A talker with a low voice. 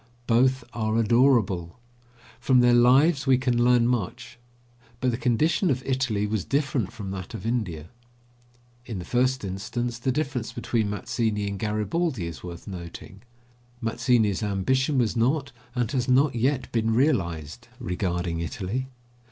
Yes: low, 120 Hz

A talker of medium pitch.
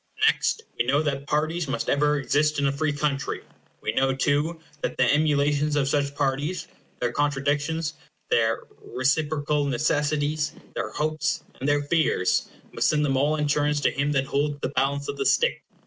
Yes: medium, 145 Hz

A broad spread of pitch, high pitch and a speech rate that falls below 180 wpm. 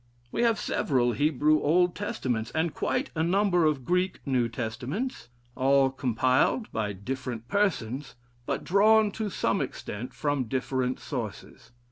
No: wide, 6.4 semitones; medium, 140 Hz; slow, 135 wpm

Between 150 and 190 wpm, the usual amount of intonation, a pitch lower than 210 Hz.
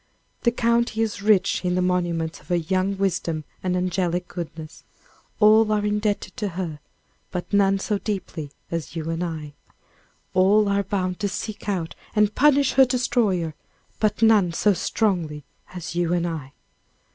Yes: average, 160 wpm; average, 3.7 semitones; high, 190 Hz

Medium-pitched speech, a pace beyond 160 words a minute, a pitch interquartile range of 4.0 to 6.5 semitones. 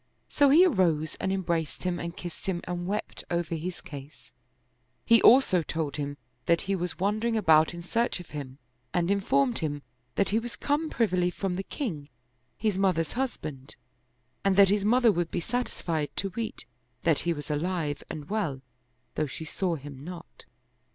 Yes: medium, 180 Hz; average, 180 wpm; average, 4.7 semitones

